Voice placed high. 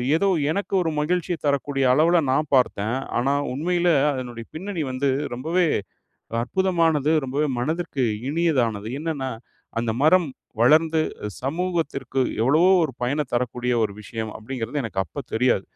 No: medium, 140 Hz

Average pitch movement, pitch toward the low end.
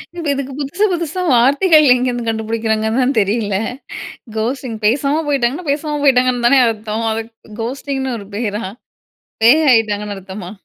No: average, 4.1 semitones; high, 245 Hz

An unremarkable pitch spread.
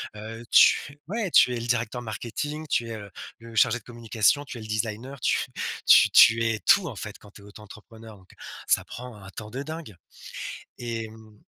No: narrow, 2.3 semitones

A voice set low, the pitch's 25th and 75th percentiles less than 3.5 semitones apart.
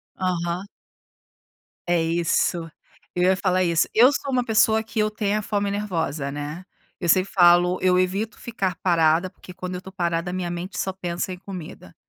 No: medium, 185 Hz; narrow, 2.6 semitones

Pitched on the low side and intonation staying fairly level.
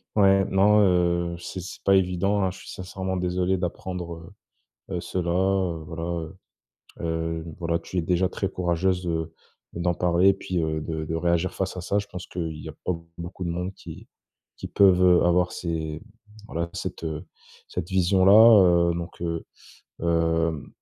Yes: very low, 90 Hz; narrow, 1.9 semitones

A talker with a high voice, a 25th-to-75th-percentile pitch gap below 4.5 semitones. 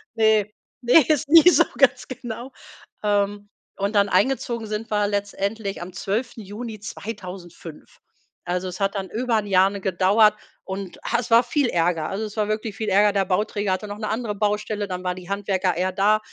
Yes: high, 205 Hz; narrow, 2.4 semitones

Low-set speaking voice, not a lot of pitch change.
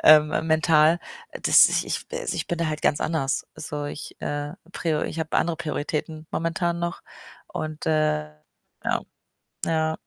No: medium, 155 Hz; narrow, 1.6 semitones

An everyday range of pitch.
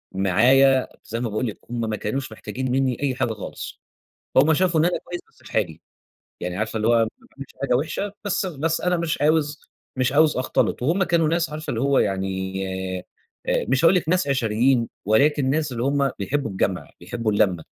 No: wide, 5.7 semitones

